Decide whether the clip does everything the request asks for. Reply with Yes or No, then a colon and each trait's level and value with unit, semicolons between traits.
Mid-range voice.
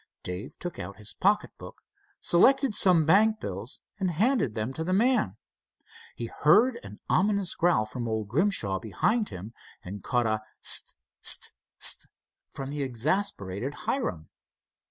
Yes: medium, 145 Hz